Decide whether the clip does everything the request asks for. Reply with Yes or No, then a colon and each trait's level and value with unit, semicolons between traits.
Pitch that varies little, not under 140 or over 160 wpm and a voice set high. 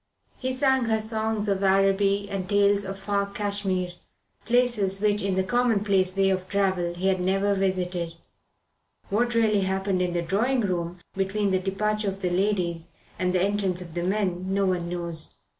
No: narrow, 2.0 semitones; average, 175 wpm; high, 195 Hz